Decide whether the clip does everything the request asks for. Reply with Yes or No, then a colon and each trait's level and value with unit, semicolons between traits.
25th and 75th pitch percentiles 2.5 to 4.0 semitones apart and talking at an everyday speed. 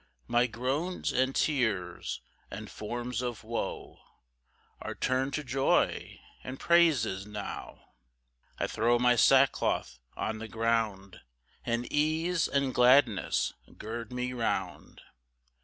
No: average, 3.3 semitones; slow, 115 wpm